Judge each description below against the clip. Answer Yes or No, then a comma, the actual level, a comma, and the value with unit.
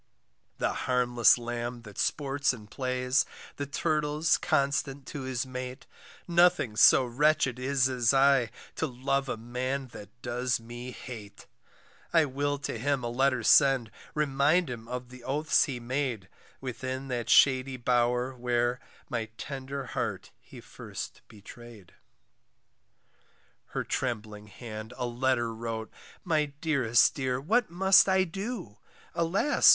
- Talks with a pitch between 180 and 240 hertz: No, low, 130 Hz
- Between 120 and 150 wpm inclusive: Yes, slow, 135 wpm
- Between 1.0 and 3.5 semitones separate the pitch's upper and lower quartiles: Yes, average, 2.8 semitones